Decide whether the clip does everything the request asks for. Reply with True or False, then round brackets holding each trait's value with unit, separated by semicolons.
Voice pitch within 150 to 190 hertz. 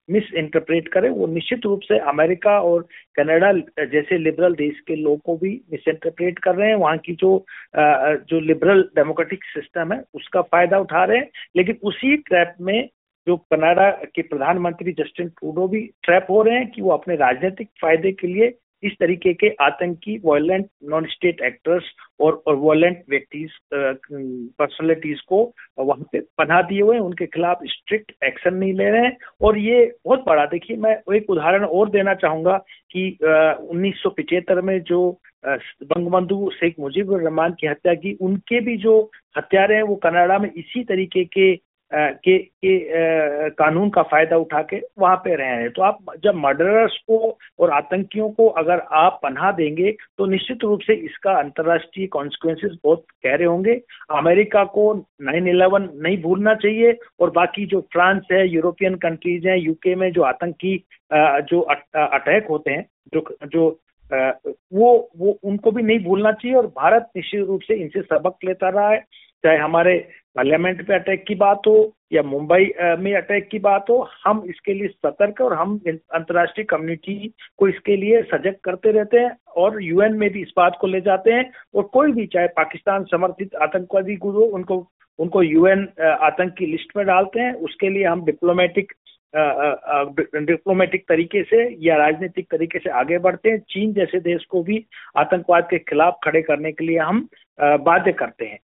True (185 Hz)